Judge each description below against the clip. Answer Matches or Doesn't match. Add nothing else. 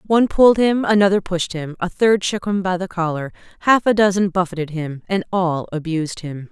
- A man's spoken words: Doesn't match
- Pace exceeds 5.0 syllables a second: Matches